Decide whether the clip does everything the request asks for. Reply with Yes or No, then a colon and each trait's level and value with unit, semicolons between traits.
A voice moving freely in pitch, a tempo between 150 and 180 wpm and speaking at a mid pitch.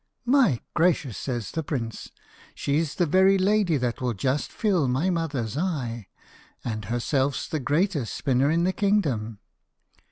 No: wide, 6.6 semitones; average, 140 wpm; medium, 145 Hz